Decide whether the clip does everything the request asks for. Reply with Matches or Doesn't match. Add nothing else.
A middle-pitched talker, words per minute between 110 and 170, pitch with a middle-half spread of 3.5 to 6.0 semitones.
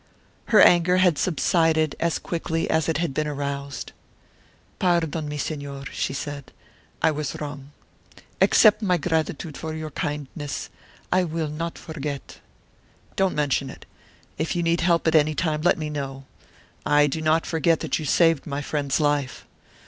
Doesn't match